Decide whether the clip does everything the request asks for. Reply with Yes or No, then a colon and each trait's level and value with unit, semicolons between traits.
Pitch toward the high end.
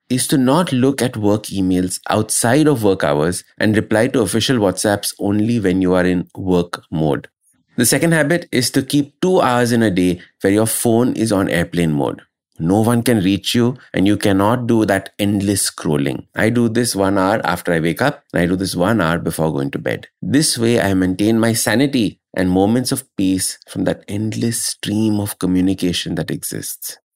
No: low, 105 Hz